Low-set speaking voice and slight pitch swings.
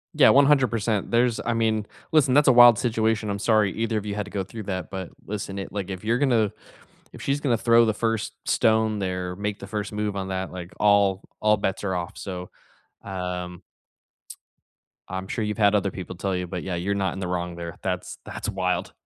No: low, 100 Hz; average, 3.0 semitones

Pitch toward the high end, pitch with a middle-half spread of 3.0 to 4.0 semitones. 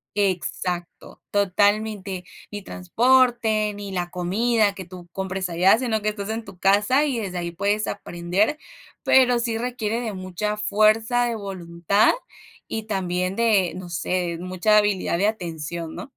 Yes: high, 200 Hz; average, 3.3 semitones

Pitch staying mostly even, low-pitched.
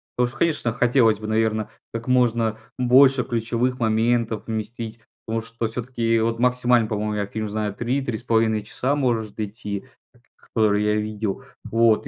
Yes: narrow, 2.0 semitones; low, 115 Hz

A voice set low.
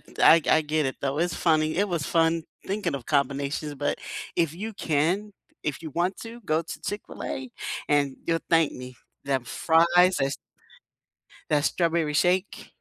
No: medium, 160 Hz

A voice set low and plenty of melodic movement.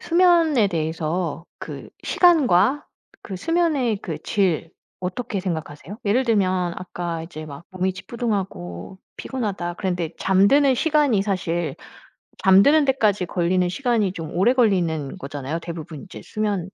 No: high, 190 Hz; wide, 5.9 semitones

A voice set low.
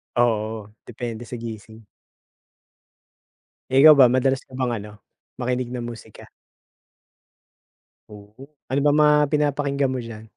Yes: low, 120 Hz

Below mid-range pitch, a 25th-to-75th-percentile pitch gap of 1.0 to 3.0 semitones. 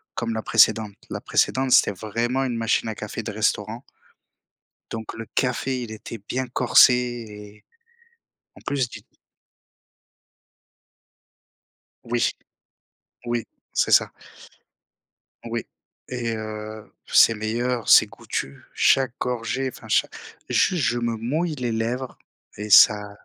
Yes: low, 115 Hz; narrow, 2.5 semitones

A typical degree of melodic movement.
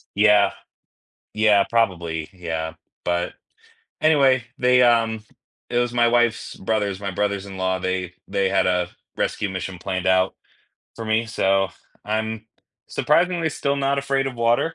Yes: average, 4.3 semitones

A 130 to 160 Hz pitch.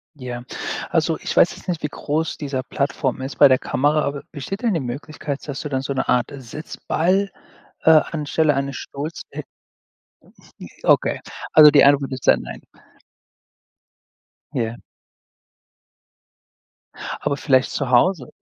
Yes: medium, 140 Hz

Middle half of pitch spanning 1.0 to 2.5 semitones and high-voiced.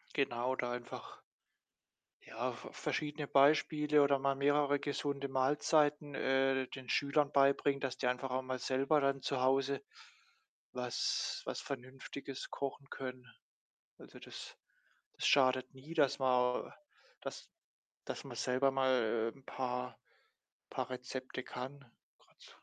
No: narrow, 1.6 semitones; low, 135 Hz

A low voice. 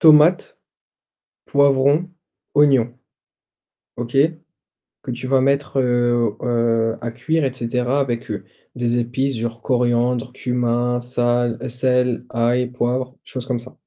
Yes: low, 125 Hz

